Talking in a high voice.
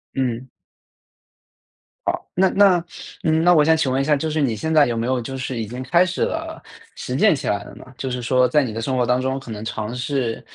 No: low, 130 Hz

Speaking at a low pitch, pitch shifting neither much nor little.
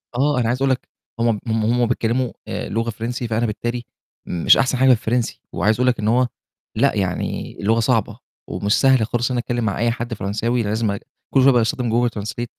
No: low, 115 Hz; narrow, 2.1 semitones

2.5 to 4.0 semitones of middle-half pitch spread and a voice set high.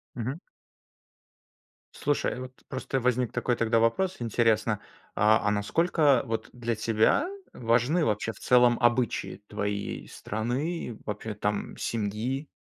No: average, 2.9 semitones; low, 115 Hz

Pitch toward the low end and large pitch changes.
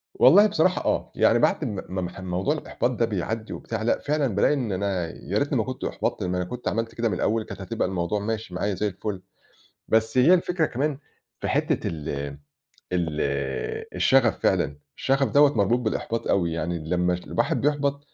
Yes: low, 110 Hz; wide, 6.4 semitones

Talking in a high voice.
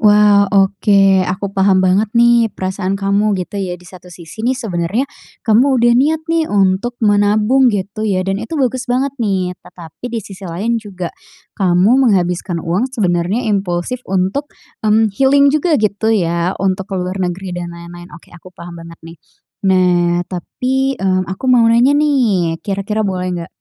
Yes: high, 200 Hz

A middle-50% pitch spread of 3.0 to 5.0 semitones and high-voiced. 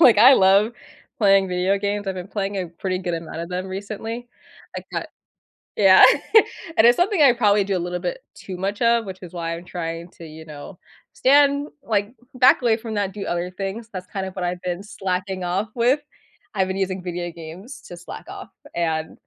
Yes: average, 3.6 semitones; high, 195 Hz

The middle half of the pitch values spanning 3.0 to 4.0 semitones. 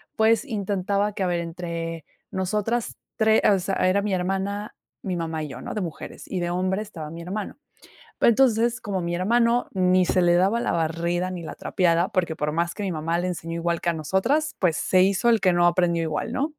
Yes: average, 3.5 semitones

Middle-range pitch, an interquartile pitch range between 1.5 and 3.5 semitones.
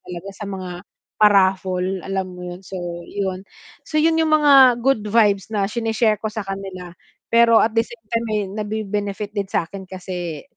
No: high, 200 Hz; average, 3.0 semitones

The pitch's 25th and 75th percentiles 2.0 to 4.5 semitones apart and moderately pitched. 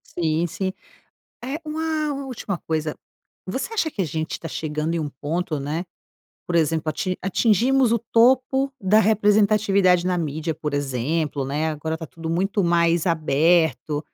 No: average, 5.2 semitones; medium, 170 Hz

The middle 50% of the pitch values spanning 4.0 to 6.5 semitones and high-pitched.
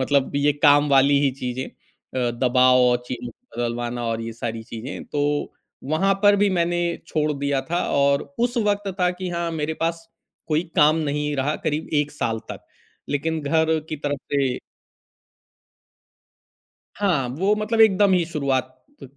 No: average, 4.6 semitones; medium, 145 Hz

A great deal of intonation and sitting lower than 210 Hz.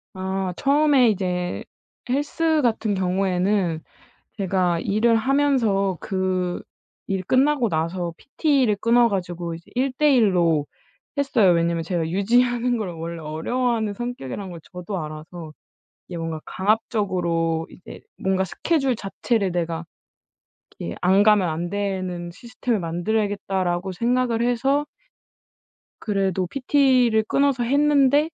Yes: wide, 5.7 semitones; high, 195 Hz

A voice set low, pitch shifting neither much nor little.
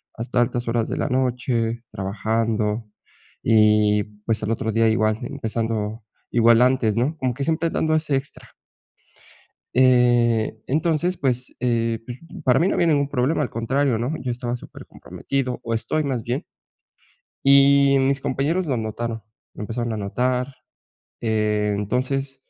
Yes: low, 120 Hz; average, 3.3 semitones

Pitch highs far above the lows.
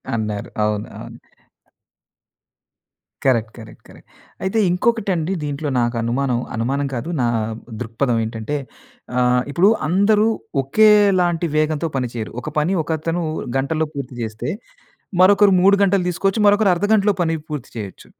Yes: wide, 7.8 semitones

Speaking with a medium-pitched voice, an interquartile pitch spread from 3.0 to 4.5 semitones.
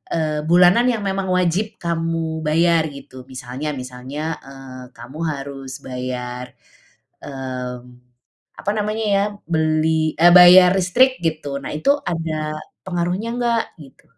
No: medium, 160 Hz; average, 5.0 semitones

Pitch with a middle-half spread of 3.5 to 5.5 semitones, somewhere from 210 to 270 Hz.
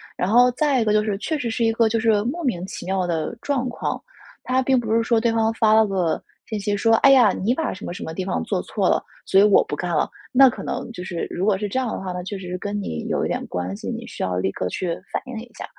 Yes: average, 4.4 semitones; high, 215 Hz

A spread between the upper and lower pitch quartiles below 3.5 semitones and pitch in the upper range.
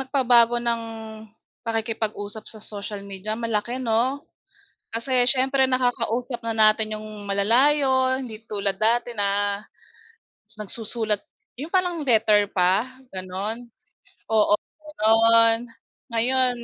Yes: average, 2.7 semitones; high, 225 Hz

